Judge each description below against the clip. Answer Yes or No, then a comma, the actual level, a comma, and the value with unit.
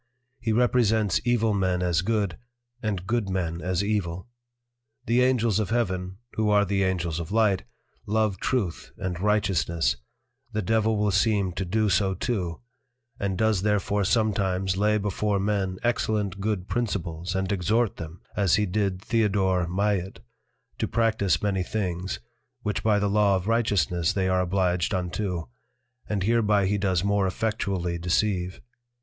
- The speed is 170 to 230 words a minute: No, average, 150 wpm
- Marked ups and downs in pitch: No, average, 2.7 semitones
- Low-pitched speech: Yes, low, 100 Hz